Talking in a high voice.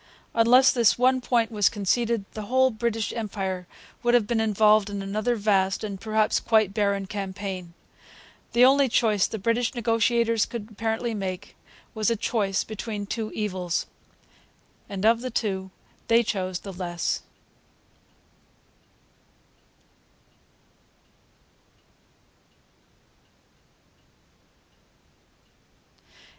Yes: high, 215 Hz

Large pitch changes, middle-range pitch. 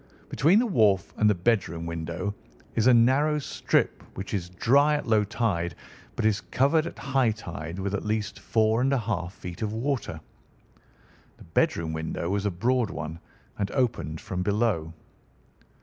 No: wide, 5.8 semitones; low, 105 Hz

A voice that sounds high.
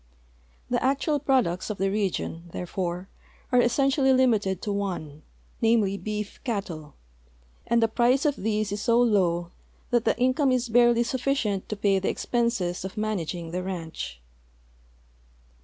Yes: high, 210 Hz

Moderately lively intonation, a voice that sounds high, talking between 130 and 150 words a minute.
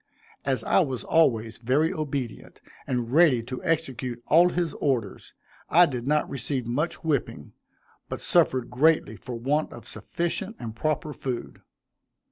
No: average, 4.7 semitones; low, 135 Hz; average, 140 wpm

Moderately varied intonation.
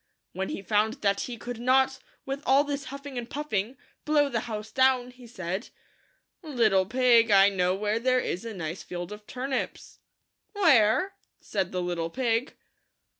Yes: average, 4.9 semitones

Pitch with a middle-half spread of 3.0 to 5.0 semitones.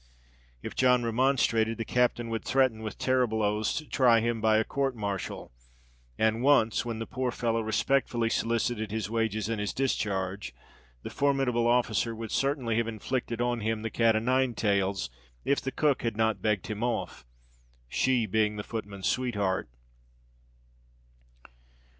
No: narrow, 2.4 semitones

